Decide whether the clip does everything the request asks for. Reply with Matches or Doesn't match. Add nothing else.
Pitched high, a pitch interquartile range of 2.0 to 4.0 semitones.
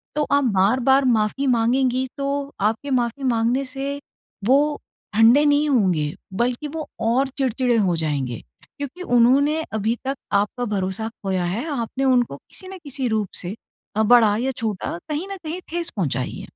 Doesn't match